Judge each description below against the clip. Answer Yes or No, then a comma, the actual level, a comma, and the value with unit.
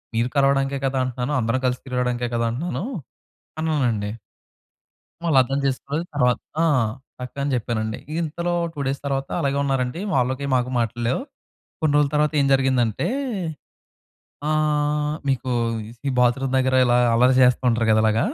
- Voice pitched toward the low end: Yes, low, 130 Hz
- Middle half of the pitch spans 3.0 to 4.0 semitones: No, narrow, 2.6 semitones